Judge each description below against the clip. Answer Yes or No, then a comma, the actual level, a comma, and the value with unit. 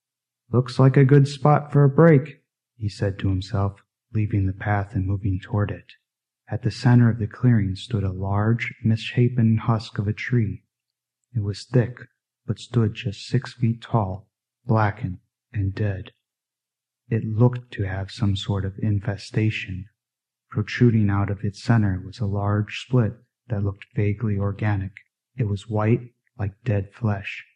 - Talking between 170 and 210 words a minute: No, average, 155 wpm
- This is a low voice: Yes, low, 110 Hz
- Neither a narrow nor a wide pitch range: Yes, average, 3.2 semitones